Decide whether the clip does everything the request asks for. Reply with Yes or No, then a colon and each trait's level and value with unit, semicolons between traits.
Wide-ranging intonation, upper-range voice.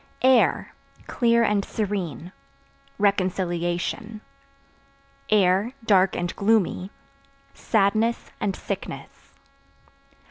No: average, 3.3 semitones; high, 200 Hz